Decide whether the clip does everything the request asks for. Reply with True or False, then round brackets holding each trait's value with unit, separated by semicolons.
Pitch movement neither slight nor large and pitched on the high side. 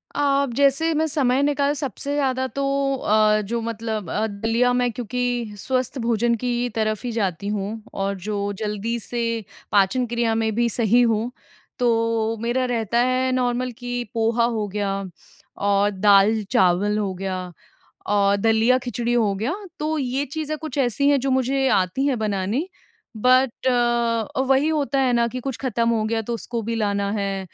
True (3.5 semitones; 235 Hz)